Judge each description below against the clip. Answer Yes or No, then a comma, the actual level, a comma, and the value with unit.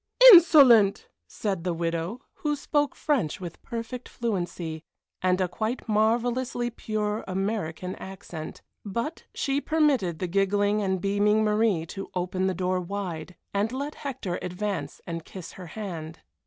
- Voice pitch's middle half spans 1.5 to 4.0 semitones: No, average, 4.4 semitones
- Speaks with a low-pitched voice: No, high, 200 Hz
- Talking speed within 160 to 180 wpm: No, average, 140 wpm